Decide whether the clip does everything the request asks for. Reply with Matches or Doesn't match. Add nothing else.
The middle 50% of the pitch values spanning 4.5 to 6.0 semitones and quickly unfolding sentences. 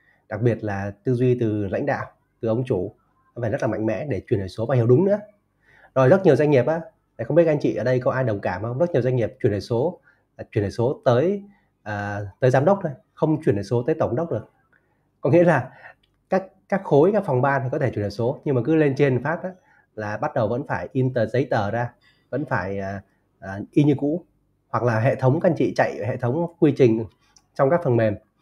Matches